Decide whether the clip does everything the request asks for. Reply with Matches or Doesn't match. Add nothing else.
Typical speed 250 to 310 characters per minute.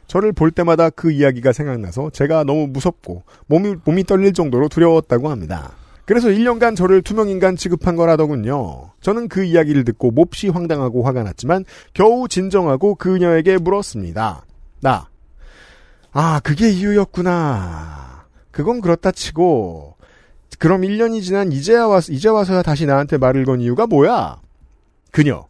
Doesn't match